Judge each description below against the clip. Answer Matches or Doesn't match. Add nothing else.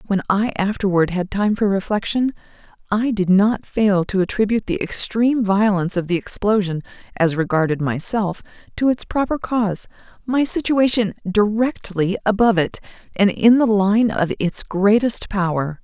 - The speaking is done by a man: Doesn't match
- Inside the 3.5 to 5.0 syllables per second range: Matches